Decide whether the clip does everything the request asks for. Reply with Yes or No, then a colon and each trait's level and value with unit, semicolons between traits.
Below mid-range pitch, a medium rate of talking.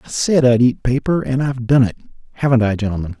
No: low, 125 Hz; fast, 225 wpm